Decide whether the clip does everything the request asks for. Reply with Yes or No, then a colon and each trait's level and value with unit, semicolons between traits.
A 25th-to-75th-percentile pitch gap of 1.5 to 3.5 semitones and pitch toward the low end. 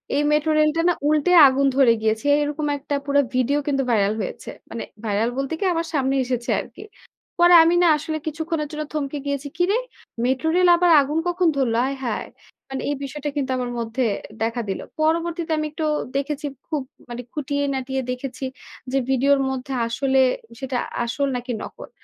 No: average, 3.1 semitones; very high, 280 Hz